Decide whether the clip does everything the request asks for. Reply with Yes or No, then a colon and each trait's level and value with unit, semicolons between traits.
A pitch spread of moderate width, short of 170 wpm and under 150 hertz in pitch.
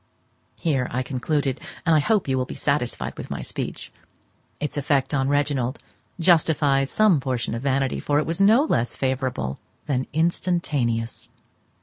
Yes: average, 3.4 semitones; average, 150 wpm; medium, 140 Hz